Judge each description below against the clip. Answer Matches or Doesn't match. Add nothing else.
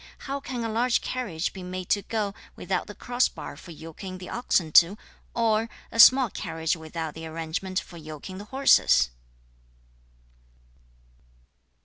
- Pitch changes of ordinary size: Doesn't match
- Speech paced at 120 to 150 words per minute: Matches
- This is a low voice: Doesn't match